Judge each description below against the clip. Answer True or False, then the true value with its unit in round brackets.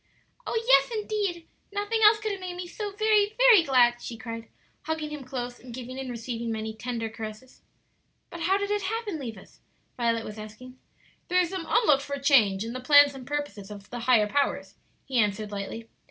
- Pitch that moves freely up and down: True (8.1 semitones)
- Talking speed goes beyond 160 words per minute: True (190 wpm)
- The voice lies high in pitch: True (260 Hz)